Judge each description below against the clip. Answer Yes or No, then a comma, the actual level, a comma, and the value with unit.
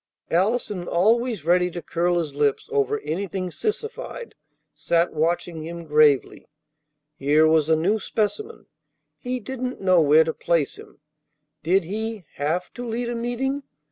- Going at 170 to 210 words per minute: No, average, 140 wpm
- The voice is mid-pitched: Yes, medium, 180 Hz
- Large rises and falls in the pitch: Yes, wide, 6.7 semitones